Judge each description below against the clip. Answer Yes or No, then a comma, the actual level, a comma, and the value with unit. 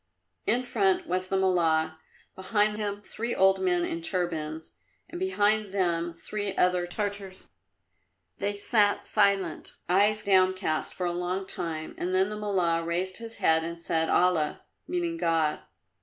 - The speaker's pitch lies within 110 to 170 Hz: No, high, 190 Hz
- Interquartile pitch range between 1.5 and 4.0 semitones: Yes, average, 3.4 semitones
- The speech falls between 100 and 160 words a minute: Yes, average, 140 wpm